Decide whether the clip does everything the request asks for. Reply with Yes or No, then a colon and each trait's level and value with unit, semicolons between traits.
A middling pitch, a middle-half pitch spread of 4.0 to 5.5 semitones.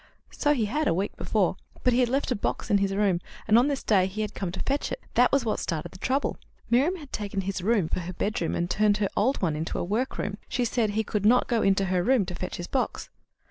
No: high, 210 Hz; average, 4.8 semitones